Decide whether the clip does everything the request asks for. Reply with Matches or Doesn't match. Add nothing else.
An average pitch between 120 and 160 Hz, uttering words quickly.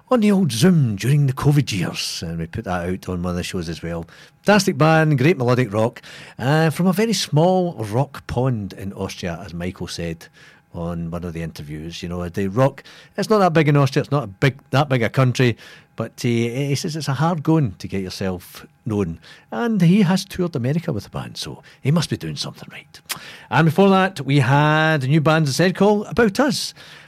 Matches